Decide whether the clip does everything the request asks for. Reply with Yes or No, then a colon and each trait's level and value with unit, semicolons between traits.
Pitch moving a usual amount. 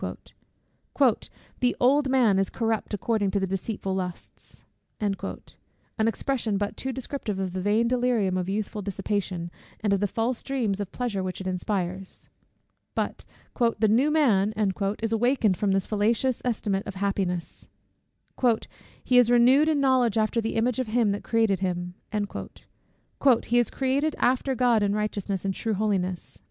Yes: average, 4.0 semitones